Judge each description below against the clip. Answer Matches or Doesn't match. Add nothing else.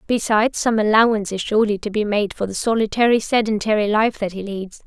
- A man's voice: Doesn't match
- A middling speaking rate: Matches